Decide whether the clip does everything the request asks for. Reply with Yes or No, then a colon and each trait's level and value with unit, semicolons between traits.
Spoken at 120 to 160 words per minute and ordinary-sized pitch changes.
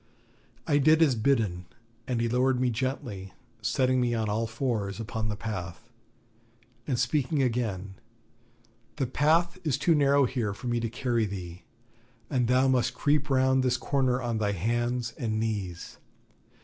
Yes: average, 155 wpm; average, 3.4 semitones